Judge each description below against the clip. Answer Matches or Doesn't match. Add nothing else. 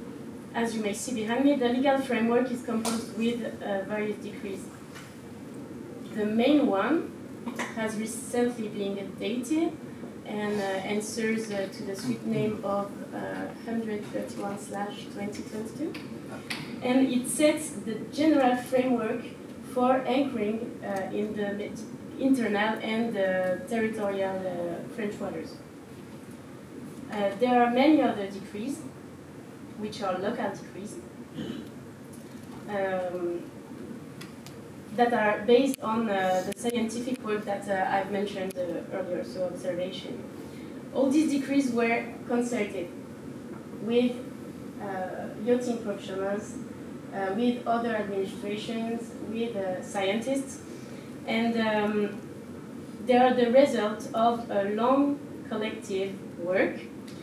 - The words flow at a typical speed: Doesn't match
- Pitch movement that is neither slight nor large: Matches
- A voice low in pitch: Doesn't match